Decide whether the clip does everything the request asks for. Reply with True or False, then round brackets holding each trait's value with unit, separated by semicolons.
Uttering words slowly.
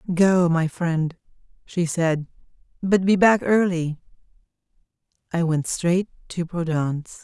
True (115 wpm)